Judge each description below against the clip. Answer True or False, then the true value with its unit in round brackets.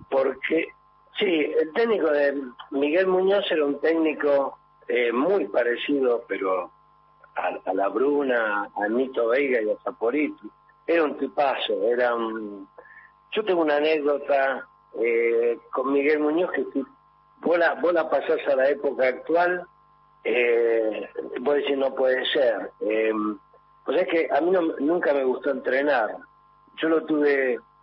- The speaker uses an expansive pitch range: True (6.7 semitones)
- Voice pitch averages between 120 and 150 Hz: True (140 Hz)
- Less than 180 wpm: True (150 wpm)